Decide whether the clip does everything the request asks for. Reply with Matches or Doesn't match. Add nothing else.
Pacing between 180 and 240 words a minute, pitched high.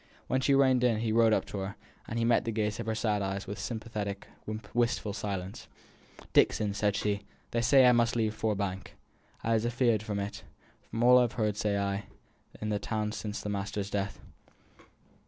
Doesn't match